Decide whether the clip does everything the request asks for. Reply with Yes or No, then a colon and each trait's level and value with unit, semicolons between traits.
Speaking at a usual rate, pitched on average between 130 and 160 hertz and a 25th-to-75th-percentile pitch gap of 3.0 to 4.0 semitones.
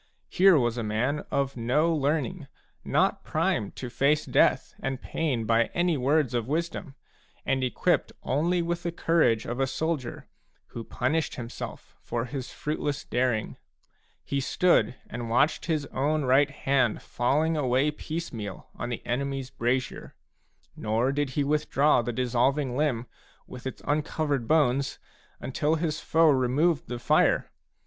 Yes: average, 145 wpm; low, 135 Hz; average, 3.7 semitones